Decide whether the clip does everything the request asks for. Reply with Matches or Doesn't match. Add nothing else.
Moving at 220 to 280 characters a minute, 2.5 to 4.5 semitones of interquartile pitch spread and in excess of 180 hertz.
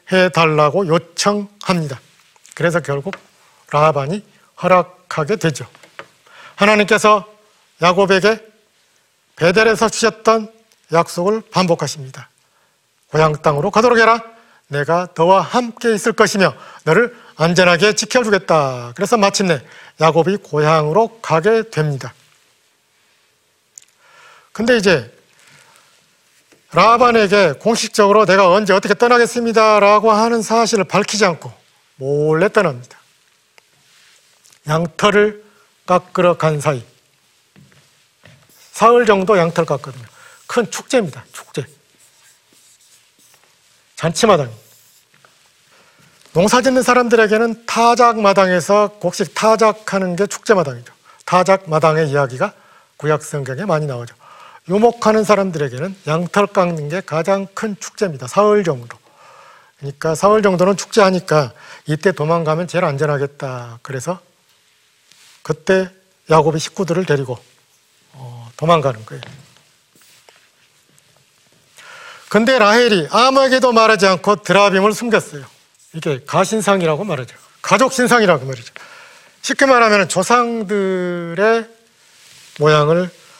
Doesn't match